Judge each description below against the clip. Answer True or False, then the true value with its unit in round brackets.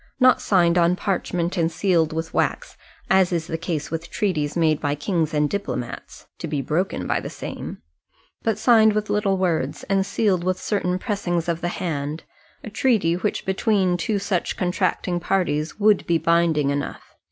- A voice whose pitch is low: False (175 Hz)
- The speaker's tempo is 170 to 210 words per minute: True (175 wpm)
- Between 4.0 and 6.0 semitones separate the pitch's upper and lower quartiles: False (3.3 semitones)